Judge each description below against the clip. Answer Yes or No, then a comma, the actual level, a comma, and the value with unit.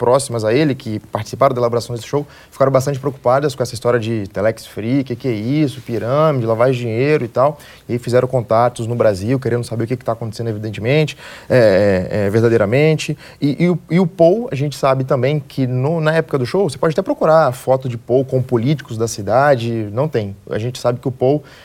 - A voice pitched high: No, low, 130 Hz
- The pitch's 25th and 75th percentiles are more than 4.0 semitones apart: No, average, 3.7 semitones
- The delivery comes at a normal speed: No, fast, 215 wpm